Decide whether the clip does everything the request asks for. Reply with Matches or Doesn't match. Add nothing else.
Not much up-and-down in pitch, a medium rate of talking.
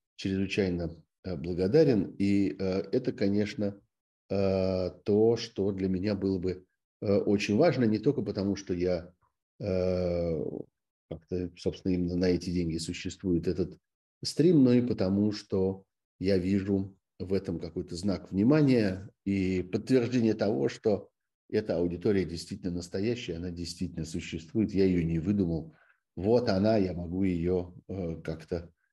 Matches